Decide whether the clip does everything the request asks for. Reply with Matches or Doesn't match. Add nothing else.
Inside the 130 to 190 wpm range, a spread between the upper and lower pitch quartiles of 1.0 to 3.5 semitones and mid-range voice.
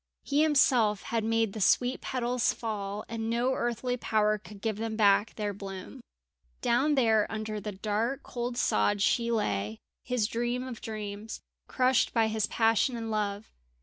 Doesn't match